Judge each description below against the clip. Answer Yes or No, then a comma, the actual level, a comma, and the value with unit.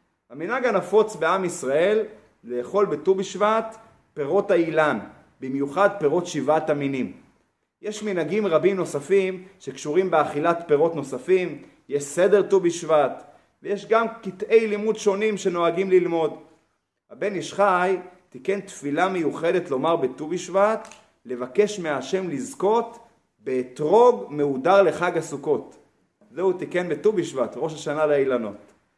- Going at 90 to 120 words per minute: Yes, average, 115 wpm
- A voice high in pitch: No, medium, 180 Hz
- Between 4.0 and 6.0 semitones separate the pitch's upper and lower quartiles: Yes, average, 4.9 semitones